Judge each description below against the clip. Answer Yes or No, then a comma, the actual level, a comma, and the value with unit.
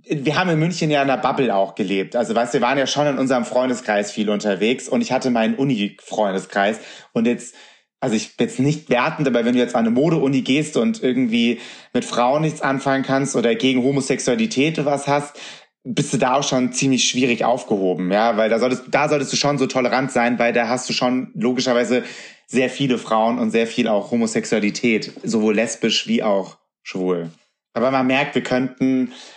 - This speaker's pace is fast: Yes, fast, 200 wpm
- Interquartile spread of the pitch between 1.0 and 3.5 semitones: Yes, average, 2.8 semitones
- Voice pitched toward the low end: Yes, low, 125 Hz